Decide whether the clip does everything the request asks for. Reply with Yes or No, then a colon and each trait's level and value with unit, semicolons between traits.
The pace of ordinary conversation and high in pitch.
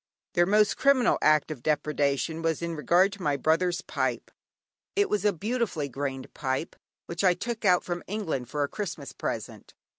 No: average, 175 wpm; medium, 170 Hz